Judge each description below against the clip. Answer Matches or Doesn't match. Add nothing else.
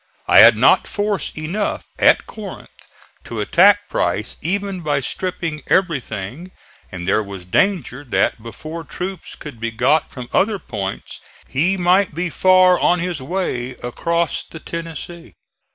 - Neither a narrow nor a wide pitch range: Doesn't match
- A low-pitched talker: Doesn't match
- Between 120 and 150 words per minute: Matches